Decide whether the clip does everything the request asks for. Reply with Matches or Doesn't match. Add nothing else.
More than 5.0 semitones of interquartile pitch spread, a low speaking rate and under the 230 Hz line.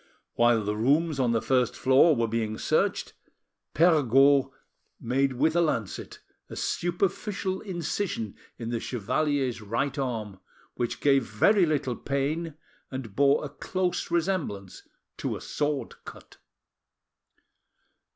Matches